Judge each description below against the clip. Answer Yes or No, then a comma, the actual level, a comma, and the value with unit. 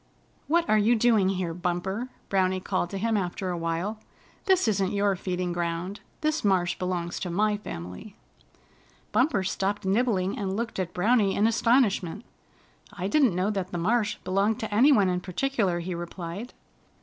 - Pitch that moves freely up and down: No, average, 3.4 semitones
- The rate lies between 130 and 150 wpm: No, average, 165 wpm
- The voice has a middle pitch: No, high, 195 Hz